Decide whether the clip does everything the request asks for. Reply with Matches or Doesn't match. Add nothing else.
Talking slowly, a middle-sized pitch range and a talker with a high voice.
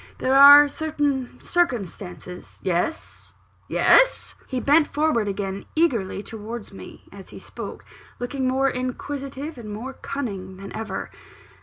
Doesn't match